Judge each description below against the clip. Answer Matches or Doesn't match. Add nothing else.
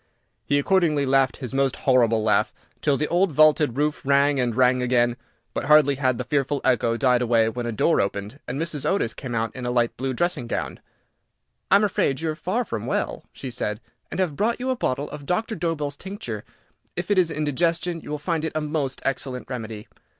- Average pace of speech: Doesn't match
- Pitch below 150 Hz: Matches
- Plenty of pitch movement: Doesn't match